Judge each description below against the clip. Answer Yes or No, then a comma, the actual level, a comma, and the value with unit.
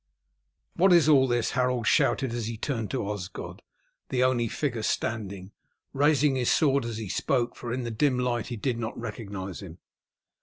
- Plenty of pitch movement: No, average, 3.3 semitones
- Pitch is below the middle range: Yes, low, 120 Hz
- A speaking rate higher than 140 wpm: Yes, average, 180 wpm